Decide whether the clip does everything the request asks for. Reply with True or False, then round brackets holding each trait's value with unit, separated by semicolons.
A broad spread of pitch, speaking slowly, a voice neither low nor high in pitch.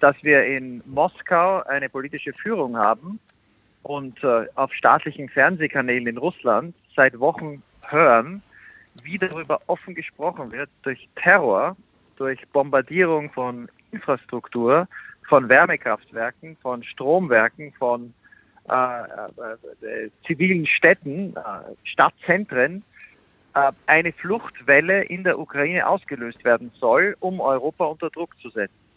True (5.8 semitones; 115 wpm; 145 Hz)